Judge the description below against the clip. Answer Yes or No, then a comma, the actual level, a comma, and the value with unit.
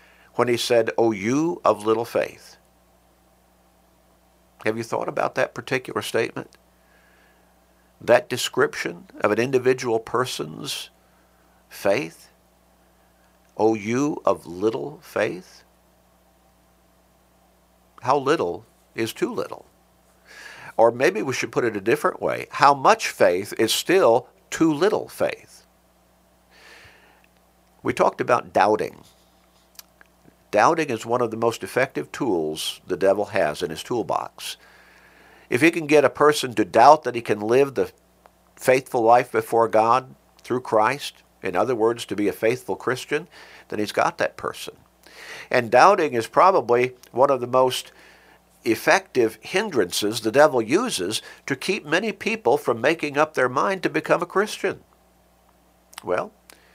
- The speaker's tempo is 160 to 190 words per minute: No, slow, 135 wpm